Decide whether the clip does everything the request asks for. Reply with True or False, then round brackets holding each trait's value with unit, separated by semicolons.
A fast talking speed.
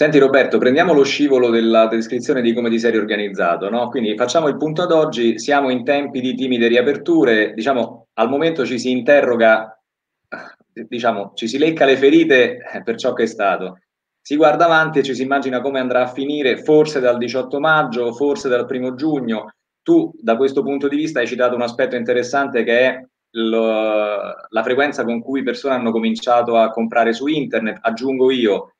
True (185 wpm)